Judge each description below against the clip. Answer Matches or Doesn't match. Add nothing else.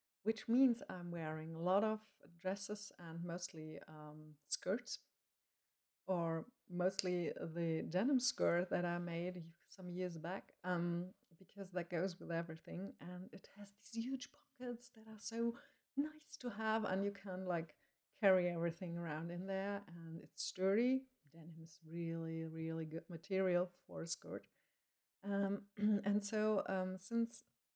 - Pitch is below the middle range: Doesn't match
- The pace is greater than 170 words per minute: Doesn't match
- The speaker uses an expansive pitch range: Doesn't match